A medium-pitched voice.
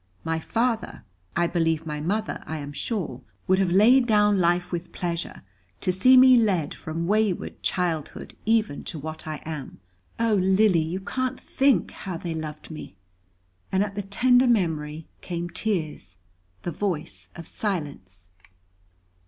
Yes: medium, 180 Hz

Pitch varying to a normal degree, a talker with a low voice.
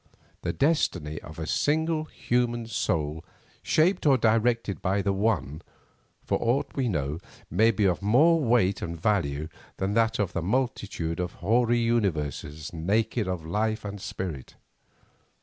No: wide, 5.9 semitones; low, 105 Hz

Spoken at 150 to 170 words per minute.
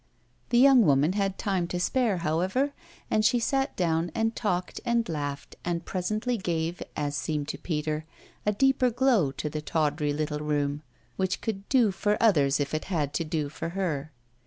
No: average, 180 wpm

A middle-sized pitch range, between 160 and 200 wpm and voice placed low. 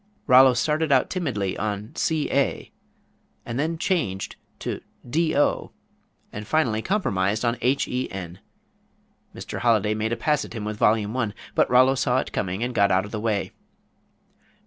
Yes: average, 4.7 semitones; average, 165 wpm; low, 115 Hz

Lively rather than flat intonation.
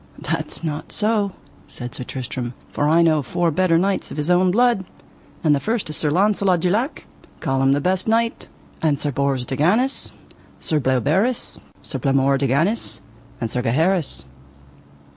Yes: wide, 6.0 semitones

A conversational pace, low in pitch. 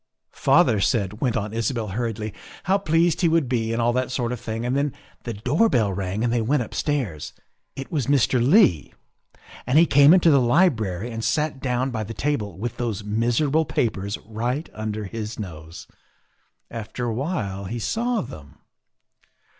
Yes: average, 180 wpm; low, 120 Hz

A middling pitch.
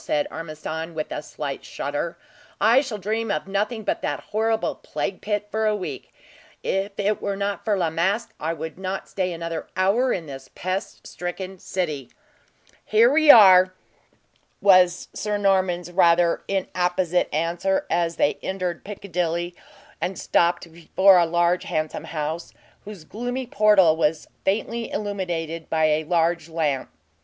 Yes: medium, 180 Hz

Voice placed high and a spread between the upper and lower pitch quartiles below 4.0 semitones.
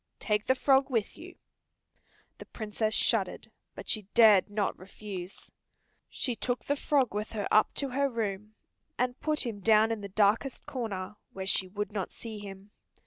Yes: high, 215 Hz; average, 3.4 semitones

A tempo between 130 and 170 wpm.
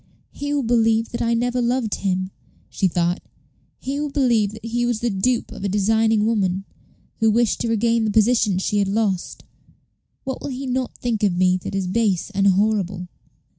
No: average, 190 wpm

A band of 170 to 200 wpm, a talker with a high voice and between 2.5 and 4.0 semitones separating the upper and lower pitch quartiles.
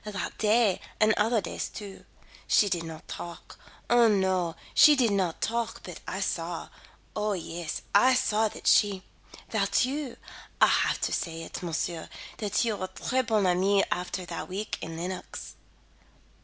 No: average, 160 wpm; high, 200 Hz; average, 3.7 semitones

